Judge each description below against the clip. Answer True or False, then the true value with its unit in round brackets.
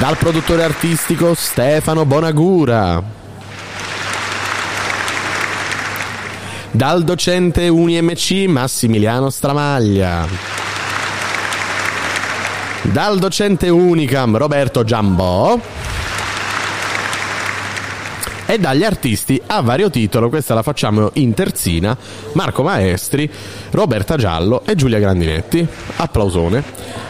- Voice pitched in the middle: False (120 Hz)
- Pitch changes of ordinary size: False (7.8 semitones)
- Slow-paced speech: True (75 wpm)